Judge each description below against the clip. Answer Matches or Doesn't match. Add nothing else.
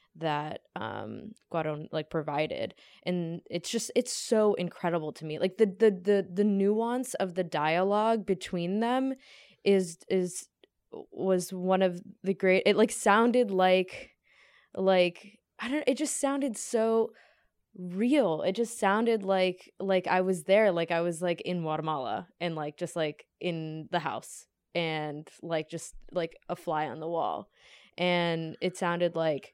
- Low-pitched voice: Doesn't match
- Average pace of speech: Matches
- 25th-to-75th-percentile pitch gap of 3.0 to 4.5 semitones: Matches